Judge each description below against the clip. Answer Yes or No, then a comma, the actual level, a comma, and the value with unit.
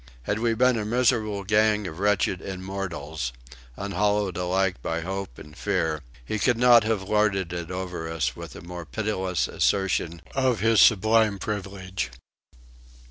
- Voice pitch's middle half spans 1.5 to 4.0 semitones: Yes, average, 3.2 semitones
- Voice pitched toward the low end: Yes, very low, 95 Hz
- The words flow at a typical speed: Yes, average, 145 wpm